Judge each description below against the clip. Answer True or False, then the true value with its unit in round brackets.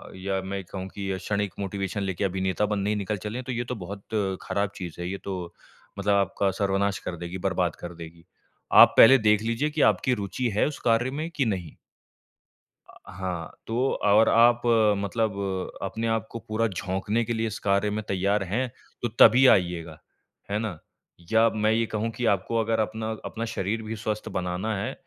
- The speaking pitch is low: True (105 Hz)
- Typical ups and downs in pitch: True (3.0 semitones)